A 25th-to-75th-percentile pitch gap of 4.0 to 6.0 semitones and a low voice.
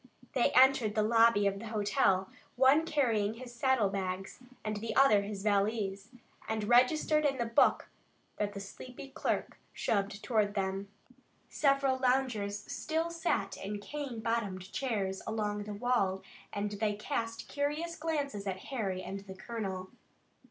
No: average, 4.5 semitones; high, 215 Hz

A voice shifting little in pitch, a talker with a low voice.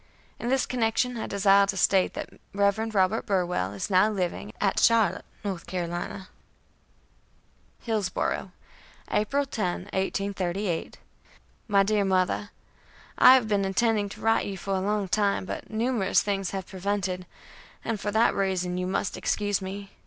No: narrow, 2.3 semitones; high, 200 Hz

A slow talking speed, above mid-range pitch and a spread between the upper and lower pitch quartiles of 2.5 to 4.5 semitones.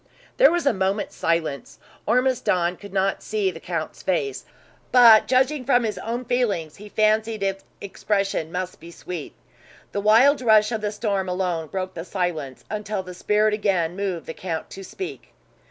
No: average, 170 wpm; high, 200 Hz; average, 3.6 semitones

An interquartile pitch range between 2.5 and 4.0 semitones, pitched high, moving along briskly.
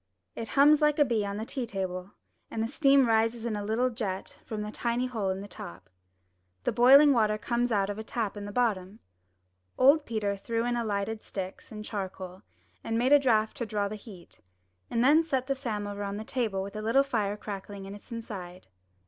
Yes: average, 3.3 semitones; high, 220 Hz; fast, 215 wpm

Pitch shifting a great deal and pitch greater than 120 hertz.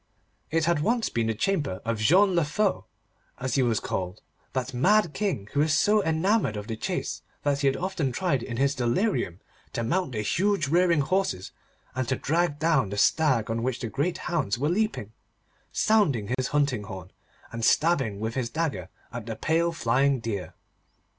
Yes: wide, 6.9 semitones; medium, 140 Hz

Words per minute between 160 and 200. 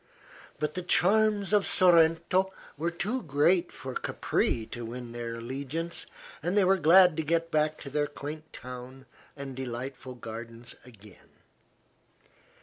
No: average, 140 wpm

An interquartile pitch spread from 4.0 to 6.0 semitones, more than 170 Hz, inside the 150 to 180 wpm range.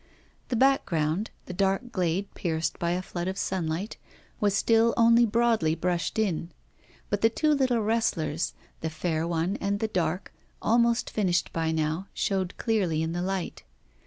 Yes: average, 5.1 semitones; high, 190 Hz; average, 160 wpm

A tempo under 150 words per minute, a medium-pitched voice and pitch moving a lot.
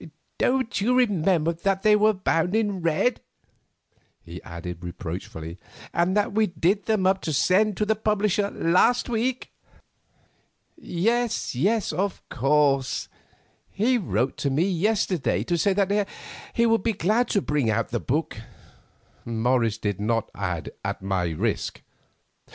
Yes: average, 140 wpm; medium, 180 Hz; wide, 8.8 semitones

